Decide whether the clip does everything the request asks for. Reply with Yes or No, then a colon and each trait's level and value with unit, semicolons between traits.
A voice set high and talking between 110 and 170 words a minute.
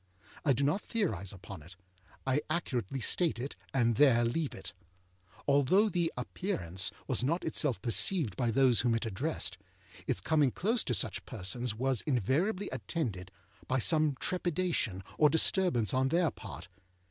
No: low, 135 Hz; average, 150 wpm